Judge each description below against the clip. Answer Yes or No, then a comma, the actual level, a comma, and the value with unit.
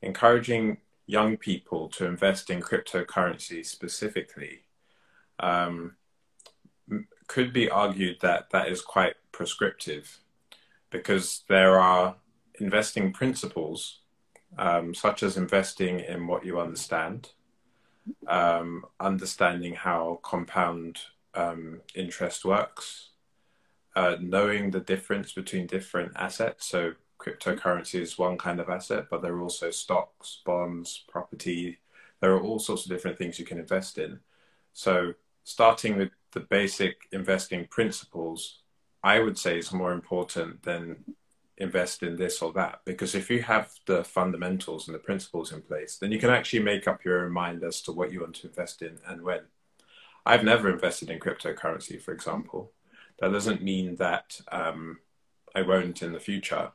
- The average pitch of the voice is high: No, very low, 90 Hz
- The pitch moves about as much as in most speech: No, narrow, 2.1 semitones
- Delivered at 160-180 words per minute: No, average, 145 wpm